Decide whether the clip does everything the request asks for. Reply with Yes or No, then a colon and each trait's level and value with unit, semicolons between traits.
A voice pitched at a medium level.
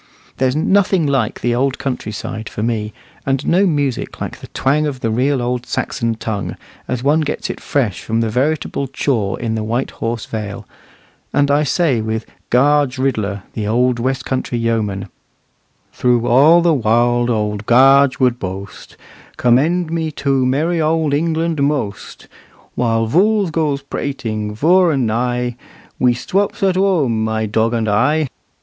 No: low, 125 Hz